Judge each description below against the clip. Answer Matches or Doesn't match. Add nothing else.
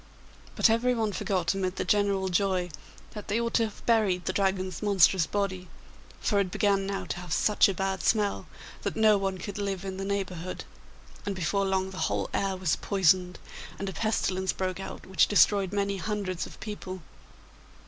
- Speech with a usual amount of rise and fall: Doesn't match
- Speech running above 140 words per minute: Matches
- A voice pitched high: Matches